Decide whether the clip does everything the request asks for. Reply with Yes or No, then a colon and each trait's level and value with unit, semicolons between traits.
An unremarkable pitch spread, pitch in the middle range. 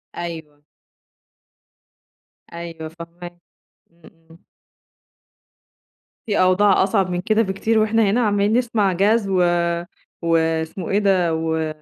Yes: average, 3.7 semitones; medium, 180 Hz